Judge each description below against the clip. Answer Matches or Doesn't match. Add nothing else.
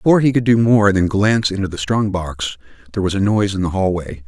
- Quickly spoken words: Matches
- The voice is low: Matches